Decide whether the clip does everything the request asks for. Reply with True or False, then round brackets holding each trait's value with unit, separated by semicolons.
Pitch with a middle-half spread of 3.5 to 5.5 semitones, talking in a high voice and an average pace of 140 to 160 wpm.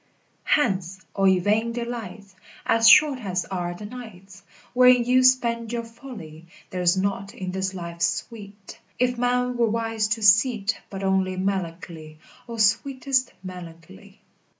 True (4.2 semitones; 205 Hz; 145 wpm)